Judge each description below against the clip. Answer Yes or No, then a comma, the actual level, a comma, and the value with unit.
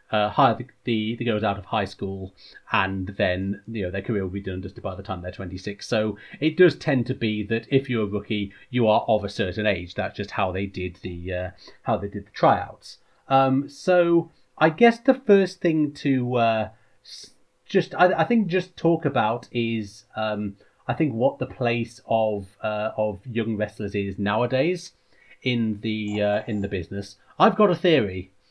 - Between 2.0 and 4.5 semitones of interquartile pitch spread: No, average, 5.0 semitones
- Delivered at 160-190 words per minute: No, average, 200 wpm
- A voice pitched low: Yes, low, 110 Hz